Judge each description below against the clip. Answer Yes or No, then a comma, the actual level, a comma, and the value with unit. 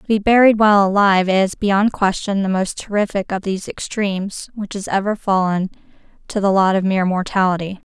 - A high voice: Yes, high, 195 Hz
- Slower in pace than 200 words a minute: Yes, average, 180 wpm